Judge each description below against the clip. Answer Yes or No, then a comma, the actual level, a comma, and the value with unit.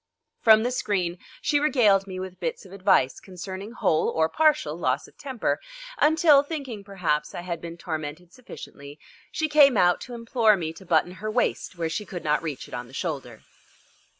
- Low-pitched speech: No, medium, 185 Hz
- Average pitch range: No, wide, 6.7 semitones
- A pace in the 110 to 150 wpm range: No, average, 185 wpm